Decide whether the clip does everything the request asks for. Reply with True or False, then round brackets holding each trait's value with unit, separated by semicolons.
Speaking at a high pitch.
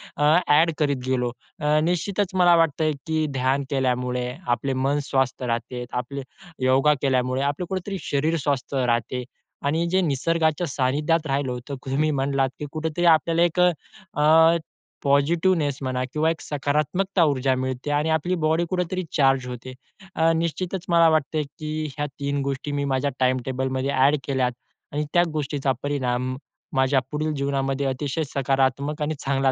False (140 Hz)